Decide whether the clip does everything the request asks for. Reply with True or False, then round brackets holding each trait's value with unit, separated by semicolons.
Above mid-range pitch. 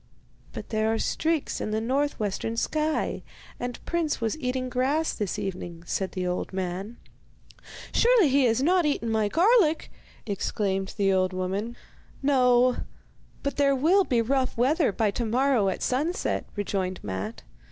True (240 Hz)